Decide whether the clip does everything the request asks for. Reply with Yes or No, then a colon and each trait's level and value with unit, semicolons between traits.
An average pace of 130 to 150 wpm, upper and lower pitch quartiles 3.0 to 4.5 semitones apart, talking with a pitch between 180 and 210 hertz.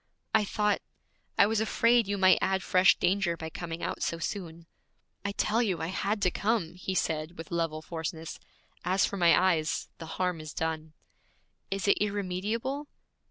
No: average, 170 wpm; average, 3.7 semitones; medium, 185 Hz